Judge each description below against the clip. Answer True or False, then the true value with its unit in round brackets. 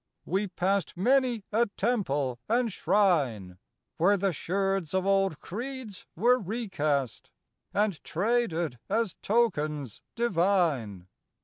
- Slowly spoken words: True (105 wpm)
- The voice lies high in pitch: True (195 Hz)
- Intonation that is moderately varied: False (6.3 semitones)